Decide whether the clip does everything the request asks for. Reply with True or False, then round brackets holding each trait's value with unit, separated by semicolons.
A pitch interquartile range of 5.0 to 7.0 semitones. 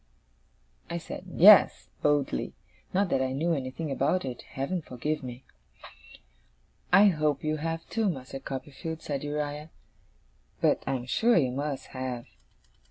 False (3.7 semitones)